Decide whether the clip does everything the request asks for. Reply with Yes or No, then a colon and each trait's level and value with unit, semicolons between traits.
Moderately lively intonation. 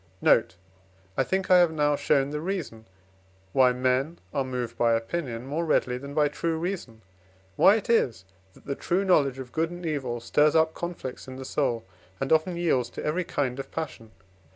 Yes: average, 4.7 semitones